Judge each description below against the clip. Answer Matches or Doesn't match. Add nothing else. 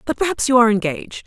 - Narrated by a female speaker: Matches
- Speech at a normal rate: Doesn't match